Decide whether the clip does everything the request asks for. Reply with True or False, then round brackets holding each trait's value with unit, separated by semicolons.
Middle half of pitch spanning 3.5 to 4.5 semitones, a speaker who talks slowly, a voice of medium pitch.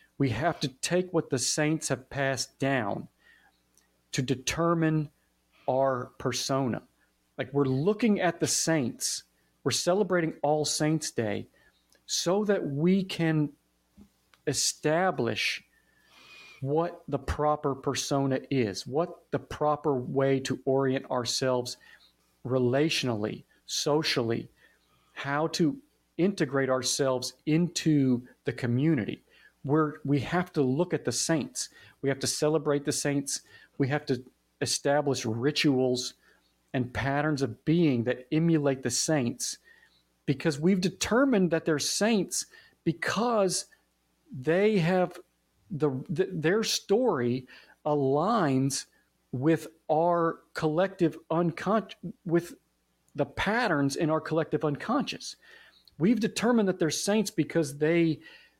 True (4.2 semitones; 115 wpm; 145 Hz)